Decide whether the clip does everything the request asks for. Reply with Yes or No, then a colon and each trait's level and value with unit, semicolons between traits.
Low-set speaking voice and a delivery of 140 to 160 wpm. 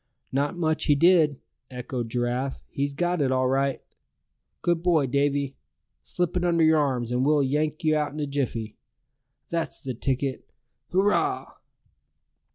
No: medium, 145 Hz; average, 150 wpm